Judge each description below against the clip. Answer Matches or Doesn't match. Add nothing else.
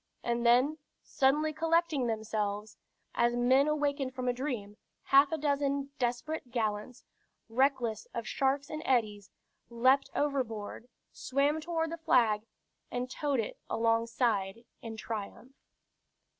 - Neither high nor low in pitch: Doesn't match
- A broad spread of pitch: Doesn't match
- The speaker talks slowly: Matches